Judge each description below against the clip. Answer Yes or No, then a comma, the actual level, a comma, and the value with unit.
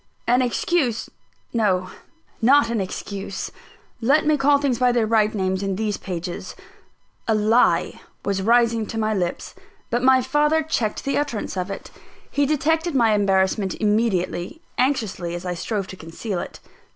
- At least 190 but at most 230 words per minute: No, average, 155 wpm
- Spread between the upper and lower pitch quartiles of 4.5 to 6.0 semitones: Yes, average, 5.1 semitones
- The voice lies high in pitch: Yes, high, 220 Hz